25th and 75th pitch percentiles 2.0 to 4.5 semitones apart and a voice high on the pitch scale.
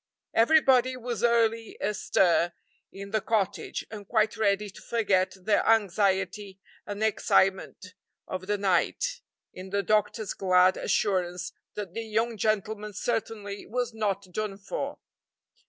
Yes: narrow, 2.6 semitones; high, 210 Hz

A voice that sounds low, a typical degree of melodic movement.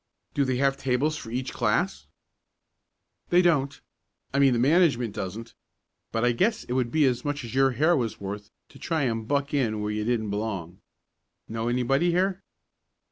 Yes: low, 125 Hz; average, 4.2 semitones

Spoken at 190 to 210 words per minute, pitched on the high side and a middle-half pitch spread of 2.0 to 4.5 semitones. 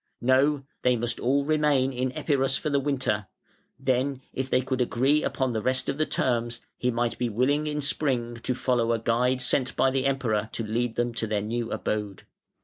No: average, 200 wpm; low, 130 Hz; narrow, 2.5 semitones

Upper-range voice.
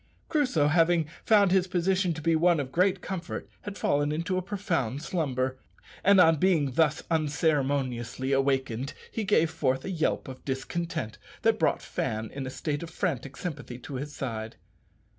No: medium, 155 Hz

